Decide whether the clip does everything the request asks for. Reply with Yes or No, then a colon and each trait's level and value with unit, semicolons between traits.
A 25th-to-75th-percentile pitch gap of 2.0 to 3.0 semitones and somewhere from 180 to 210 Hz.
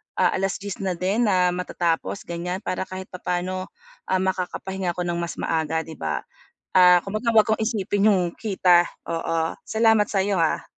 Yes: narrow, 2.4 semitones; medium, 185 Hz